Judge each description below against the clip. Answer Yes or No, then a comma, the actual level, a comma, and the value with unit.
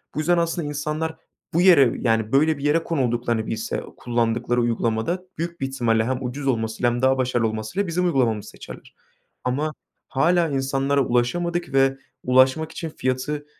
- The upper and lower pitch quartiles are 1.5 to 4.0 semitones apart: No, average, 4.8 semitones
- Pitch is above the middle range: No, low, 135 Hz